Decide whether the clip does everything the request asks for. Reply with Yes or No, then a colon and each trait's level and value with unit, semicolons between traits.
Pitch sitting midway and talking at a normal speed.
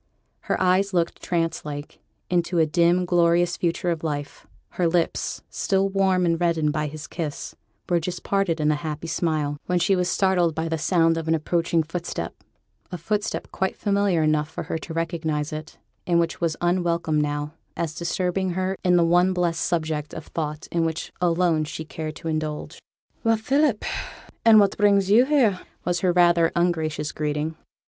Yes: medium, 170 Hz; average, 180 wpm